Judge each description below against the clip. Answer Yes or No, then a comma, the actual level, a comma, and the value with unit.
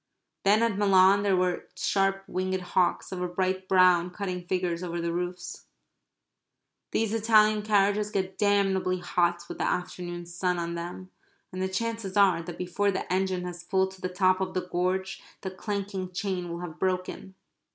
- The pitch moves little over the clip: Yes, narrow, 1.5 semitones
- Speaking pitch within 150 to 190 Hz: Yes, medium, 185 Hz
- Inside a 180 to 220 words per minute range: No, average, 170 wpm